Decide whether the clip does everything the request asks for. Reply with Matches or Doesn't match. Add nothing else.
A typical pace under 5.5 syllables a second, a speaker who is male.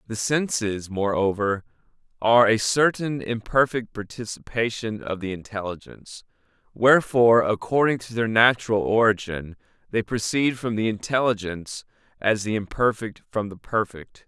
Matches